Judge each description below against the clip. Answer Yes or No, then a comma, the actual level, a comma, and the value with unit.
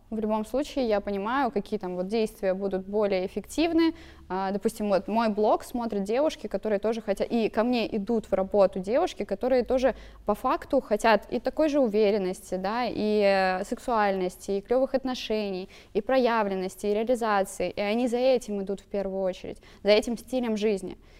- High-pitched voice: Yes, high, 210 Hz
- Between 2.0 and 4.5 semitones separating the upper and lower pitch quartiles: Yes, average, 3.6 semitones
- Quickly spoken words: Yes, fast, 165 wpm